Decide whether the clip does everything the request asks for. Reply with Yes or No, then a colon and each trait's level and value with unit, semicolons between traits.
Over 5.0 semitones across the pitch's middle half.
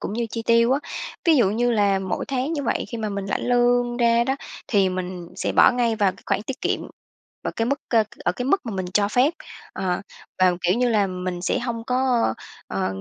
No: average, 4.3 semitones